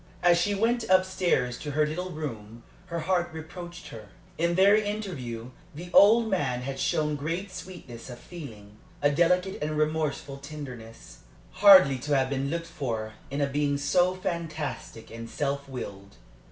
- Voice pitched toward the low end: No, medium, 155 Hz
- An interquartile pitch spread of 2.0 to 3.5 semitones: No, average, 5.3 semitones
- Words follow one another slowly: No, average, 160 wpm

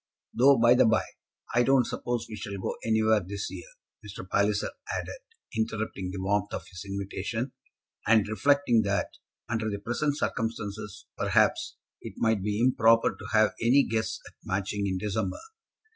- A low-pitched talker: Yes, low, 110 Hz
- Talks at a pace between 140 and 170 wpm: Yes, average, 160 wpm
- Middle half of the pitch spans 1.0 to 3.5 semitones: Yes, narrow, 2.5 semitones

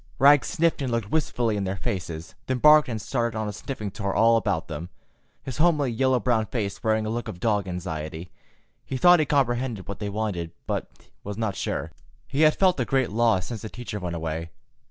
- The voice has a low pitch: Yes, low, 110 Hz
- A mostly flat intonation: No, average, 5.1 semitones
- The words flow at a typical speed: No, fast, 210 wpm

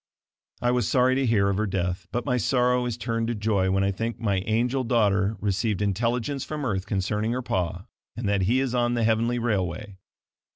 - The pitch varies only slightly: No, average, 3.6 semitones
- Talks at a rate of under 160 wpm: No, fast, 205 wpm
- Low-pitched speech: Yes, low, 110 Hz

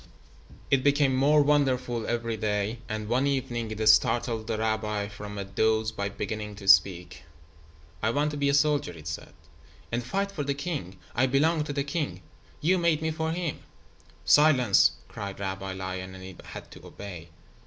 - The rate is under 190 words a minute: Yes, average, 175 wpm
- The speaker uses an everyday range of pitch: No, wide, 5.9 semitones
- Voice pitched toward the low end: Yes, low, 115 Hz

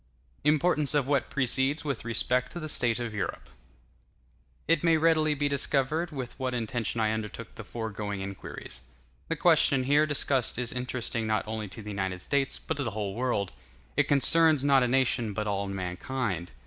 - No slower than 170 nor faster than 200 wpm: Yes, average, 175 wpm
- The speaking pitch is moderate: No, low, 125 Hz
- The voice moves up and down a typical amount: Yes, average, 4.8 semitones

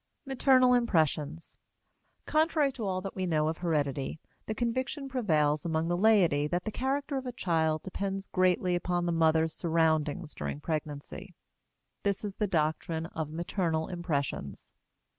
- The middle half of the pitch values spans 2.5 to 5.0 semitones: No, wide, 5.4 semitones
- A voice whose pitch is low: No, medium, 175 Hz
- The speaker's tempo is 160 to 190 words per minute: No, average, 145 wpm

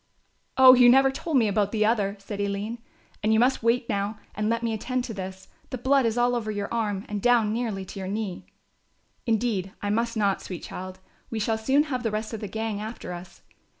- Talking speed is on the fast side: Yes, fast, 220 wpm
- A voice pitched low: No, high, 220 Hz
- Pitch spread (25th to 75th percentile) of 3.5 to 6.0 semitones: No, average, 3.0 semitones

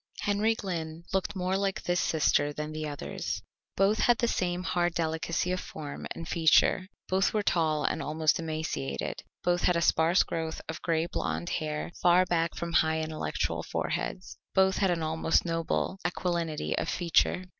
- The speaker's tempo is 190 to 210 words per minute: No, average, 165 wpm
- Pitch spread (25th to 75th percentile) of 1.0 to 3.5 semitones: Yes, narrow, 2.5 semitones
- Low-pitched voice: No, medium, 170 Hz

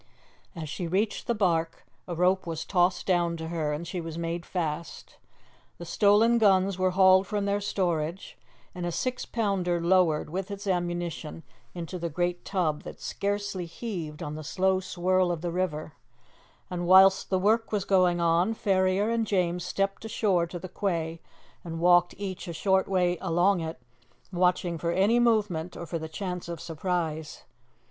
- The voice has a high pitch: No, medium, 180 Hz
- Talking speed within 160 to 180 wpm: Yes, average, 170 wpm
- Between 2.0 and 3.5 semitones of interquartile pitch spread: Yes, narrow, 2.5 semitones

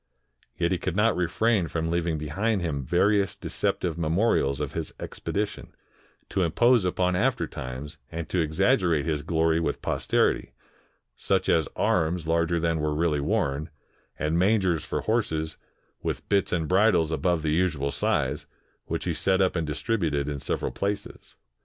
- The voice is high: No, very low, 85 Hz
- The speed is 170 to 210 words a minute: No, average, 155 wpm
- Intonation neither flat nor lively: Yes, average, 3.3 semitones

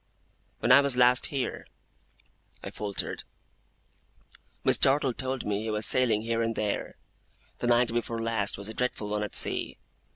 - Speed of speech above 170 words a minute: No, average, 160 wpm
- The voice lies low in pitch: Yes, low, 115 Hz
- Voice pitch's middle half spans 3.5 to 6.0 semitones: No, average, 2.9 semitones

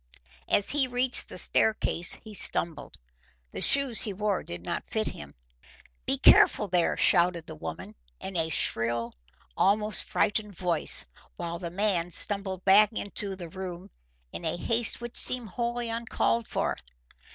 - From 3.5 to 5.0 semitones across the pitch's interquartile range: Yes, average, 4.2 semitones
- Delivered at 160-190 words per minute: No, average, 150 wpm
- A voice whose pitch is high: Yes, high, 195 Hz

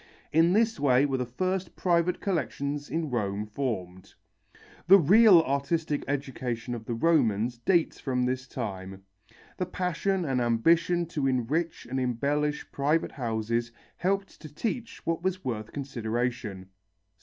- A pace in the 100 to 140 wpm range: Yes, slow, 135 wpm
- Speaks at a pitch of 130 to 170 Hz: Yes, medium, 140 Hz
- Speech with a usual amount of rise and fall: No, wide, 6.1 semitones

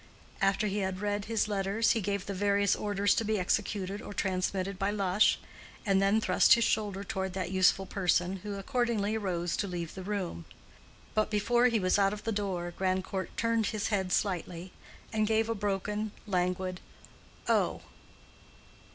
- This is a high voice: Yes, high, 200 Hz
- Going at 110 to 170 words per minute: Yes, average, 165 wpm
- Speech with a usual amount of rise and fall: No, narrow, 2.0 semitones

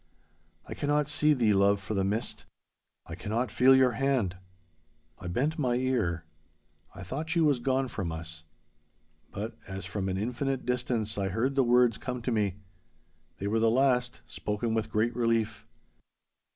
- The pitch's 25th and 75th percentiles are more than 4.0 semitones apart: Yes, average, 4.4 semitones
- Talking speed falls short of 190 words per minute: Yes, average, 165 wpm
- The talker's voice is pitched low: Yes, low, 120 Hz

